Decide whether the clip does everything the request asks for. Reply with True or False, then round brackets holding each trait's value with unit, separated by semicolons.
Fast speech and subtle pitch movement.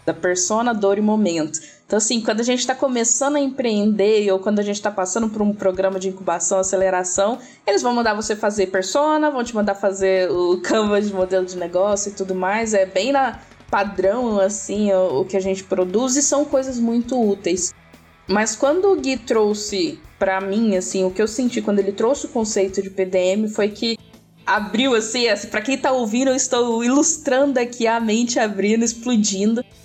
False (195 wpm; 3.9 semitones)